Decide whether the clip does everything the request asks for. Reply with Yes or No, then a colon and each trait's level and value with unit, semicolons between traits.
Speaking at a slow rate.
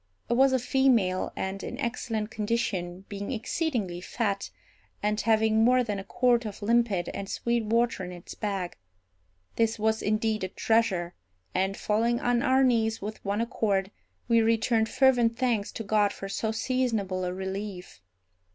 No: average, 160 wpm